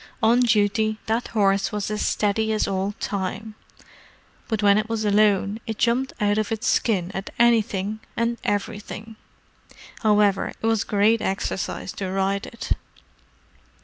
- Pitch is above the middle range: Yes, high, 210 Hz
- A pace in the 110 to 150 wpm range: Yes, average, 145 wpm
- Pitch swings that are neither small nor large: No, narrow, 1.9 semitones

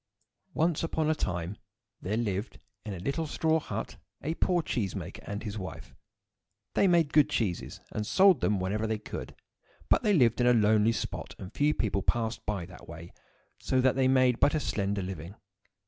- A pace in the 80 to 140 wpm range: No, average, 190 wpm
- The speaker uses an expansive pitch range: Yes, wide, 6.8 semitones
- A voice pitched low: Yes, low, 110 Hz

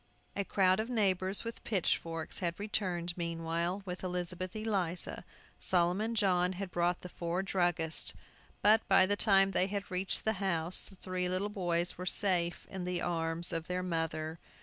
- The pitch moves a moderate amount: No, narrow, 2.2 semitones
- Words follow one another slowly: No, average, 160 wpm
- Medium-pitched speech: Yes, medium, 180 Hz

